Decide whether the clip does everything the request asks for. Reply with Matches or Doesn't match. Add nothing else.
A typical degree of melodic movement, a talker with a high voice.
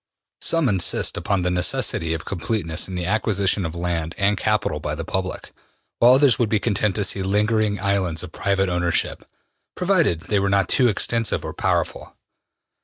Doesn't match